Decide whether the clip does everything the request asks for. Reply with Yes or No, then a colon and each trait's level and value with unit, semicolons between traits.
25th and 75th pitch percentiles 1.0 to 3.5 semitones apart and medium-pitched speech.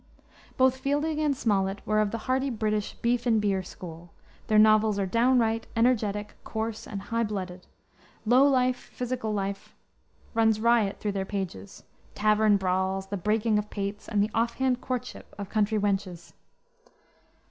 No: average, 2.9 semitones; high, 215 Hz